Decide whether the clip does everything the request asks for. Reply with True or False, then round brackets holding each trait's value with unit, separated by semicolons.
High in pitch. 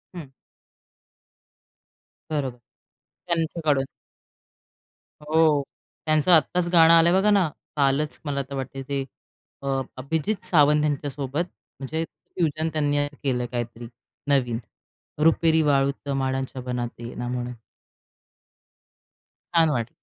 False (145 Hz)